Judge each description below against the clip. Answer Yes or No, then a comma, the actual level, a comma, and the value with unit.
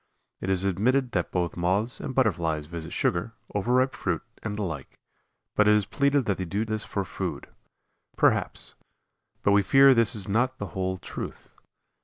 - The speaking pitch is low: Yes, low, 100 Hz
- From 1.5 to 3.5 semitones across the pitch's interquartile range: No, average, 4.8 semitones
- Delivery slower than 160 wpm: No, average, 175 wpm